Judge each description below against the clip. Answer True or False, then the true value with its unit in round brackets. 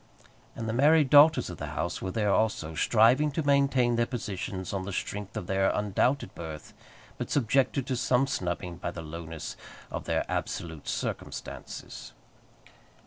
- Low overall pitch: True (105 Hz)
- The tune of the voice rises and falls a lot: True (6.8 semitones)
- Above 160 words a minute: False (155 wpm)